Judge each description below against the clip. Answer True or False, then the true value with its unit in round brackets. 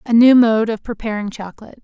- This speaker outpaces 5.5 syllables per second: True (6.4 syllables/s)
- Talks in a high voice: True (220 Hz)